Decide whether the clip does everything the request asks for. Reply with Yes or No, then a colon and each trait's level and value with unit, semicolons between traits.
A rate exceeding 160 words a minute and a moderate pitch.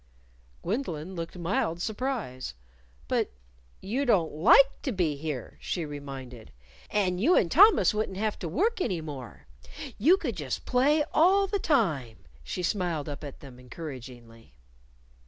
No: average, 140 wpm; medium, 175 Hz